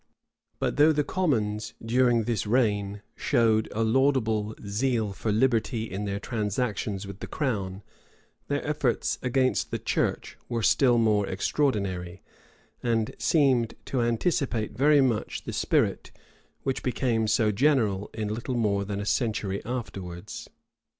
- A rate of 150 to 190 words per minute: No, slow, 135 wpm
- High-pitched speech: No, low, 115 Hz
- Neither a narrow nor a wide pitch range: Yes, average, 3.8 semitones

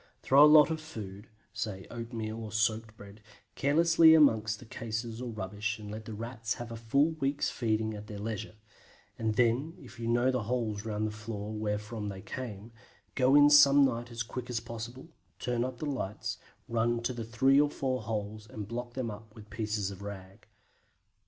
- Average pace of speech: Yes, average, 195 wpm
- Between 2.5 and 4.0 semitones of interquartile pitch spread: Yes, average, 2.9 semitones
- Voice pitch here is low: Yes, low, 115 Hz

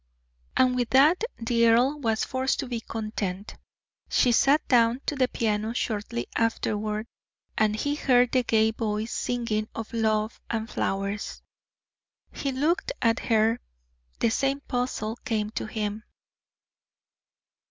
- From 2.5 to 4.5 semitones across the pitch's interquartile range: Yes, average, 2.8 semitones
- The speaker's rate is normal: No, slow, 130 wpm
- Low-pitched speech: No, high, 230 Hz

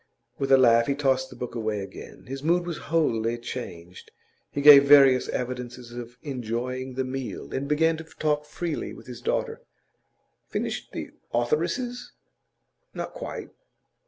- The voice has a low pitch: Yes, low, 130 Hz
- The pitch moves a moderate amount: Yes, average, 3.7 semitones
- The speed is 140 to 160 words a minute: Yes, average, 150 wpm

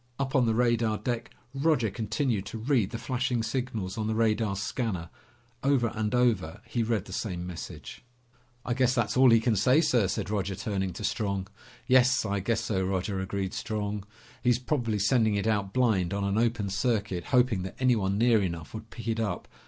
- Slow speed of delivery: No, average, 190 wpm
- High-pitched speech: No, low, 110 Hz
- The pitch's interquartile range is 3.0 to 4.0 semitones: Yes, average, 3.6 semitones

